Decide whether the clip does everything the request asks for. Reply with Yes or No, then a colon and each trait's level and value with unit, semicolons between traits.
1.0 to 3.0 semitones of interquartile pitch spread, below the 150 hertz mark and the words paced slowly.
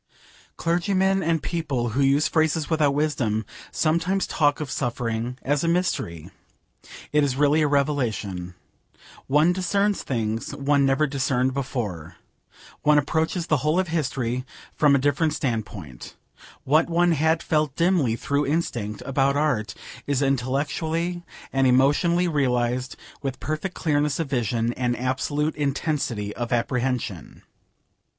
No: average, 4.2 semitones; medium, 140 Hz; slow, 130 wpm